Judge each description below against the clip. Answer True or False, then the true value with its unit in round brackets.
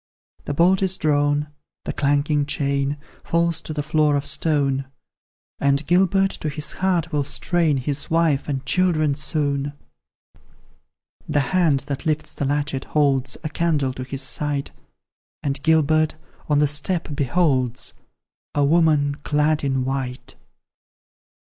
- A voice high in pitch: False (145 Hz)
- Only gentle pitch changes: True (2.3 semitones)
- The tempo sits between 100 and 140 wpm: True (135 wpm)